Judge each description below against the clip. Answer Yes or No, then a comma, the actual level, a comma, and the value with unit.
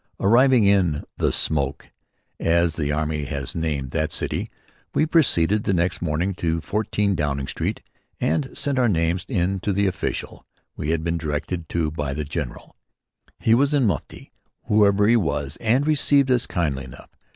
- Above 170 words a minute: No, average, 165 wpm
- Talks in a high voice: No, very low, 85 Hz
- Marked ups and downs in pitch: Yes, wide, 5.7 semitones